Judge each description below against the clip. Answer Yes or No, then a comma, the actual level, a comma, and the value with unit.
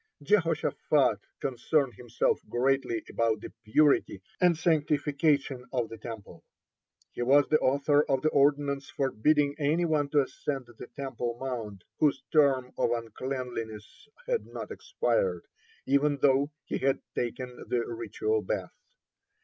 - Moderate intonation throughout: Yes, average, 3.4 semitones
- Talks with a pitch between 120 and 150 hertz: Yes, low, 135 Hz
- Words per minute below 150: Yes, slow, 135 wpm